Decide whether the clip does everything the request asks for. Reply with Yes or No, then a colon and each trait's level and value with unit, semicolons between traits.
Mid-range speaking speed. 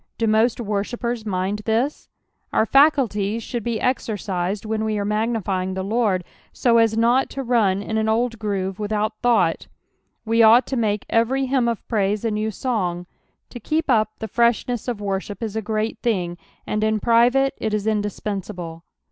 Yes: average, 175 wpm